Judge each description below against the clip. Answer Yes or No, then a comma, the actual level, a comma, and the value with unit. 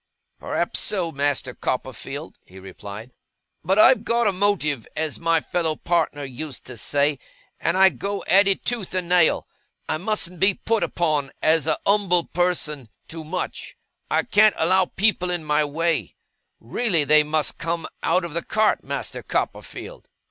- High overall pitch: No, medium, 165 Hz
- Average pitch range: Yes, average, 4.3 semitones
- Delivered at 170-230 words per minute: No, average, 160 wpm